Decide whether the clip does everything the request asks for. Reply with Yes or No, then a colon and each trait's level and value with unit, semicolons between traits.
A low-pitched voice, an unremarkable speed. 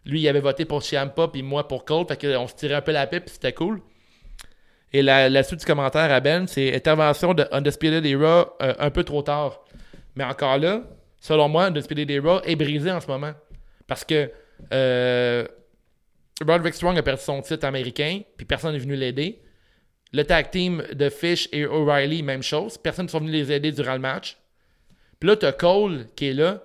No: medium, 145 Hz; average, 205 wpm